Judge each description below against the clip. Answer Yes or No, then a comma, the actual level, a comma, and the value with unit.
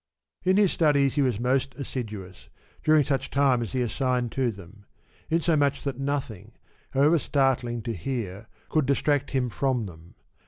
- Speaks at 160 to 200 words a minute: Yes, average, 165 wpm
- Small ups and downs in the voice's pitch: No, average, 3.6 semitones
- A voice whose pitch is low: Yes, low, 130 Hz